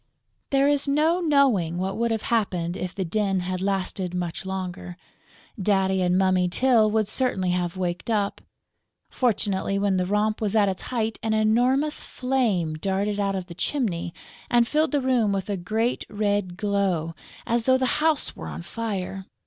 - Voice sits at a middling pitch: No, high, 200 Hz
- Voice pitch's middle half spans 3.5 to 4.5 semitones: Yes, average, 4.1 semitones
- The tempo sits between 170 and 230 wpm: Yes, average, 175 wpm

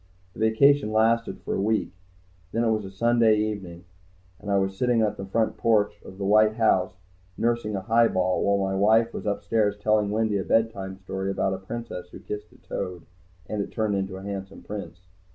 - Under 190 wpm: No, average, 200 wpm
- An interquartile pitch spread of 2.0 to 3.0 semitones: Yes, narrow, 2.5 semitones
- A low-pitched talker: Yes, low, 105 Hz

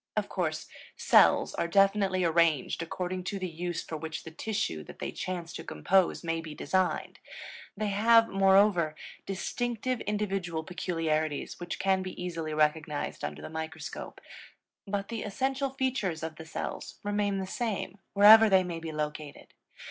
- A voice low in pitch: No, medium, 185 Hz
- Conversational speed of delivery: Yes, average, 155 wpm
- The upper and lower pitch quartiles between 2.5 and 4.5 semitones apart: Yes, average, 4.0 semitones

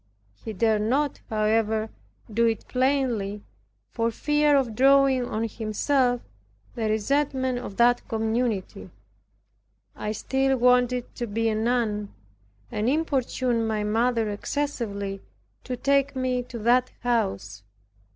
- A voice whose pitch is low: No, high, 235 Hz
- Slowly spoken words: Yes, slow, 120 wpm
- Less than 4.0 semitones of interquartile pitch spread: Yes, average, 3.1 semitones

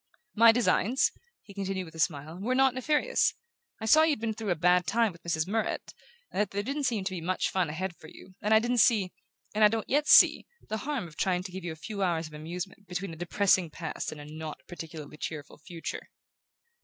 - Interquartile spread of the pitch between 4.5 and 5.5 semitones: Yes, average, 5.1 semitones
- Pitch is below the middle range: No, high, 190 Hz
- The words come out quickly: Yes, fast, 230 wpm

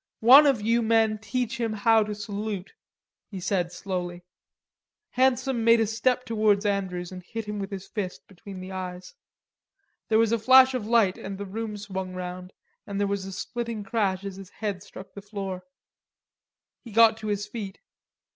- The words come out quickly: No, average, 175 wpm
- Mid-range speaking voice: No, high, 205 Hz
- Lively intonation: No, average, 2.9 semitones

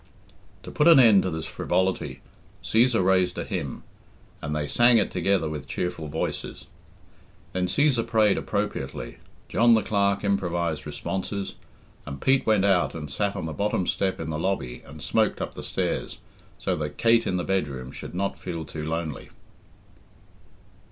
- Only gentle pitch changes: No, average, 4.7 semitones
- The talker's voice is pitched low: Yes, very low, 95 Hz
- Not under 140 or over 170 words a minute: Yes, average, 165 wpm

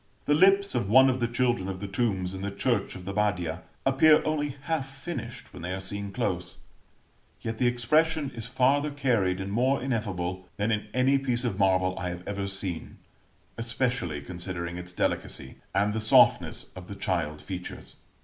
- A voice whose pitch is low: Yes, low, 105 Hz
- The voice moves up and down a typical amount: No, wide, 5.7 semitones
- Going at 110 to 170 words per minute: No, average, 180 wpm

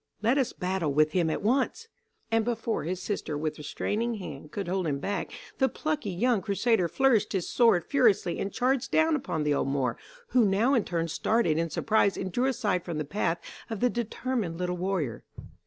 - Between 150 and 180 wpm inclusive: No, average, 195 wpm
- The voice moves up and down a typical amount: No, wide, 6.0 semitones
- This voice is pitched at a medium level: No, high, 195 Hz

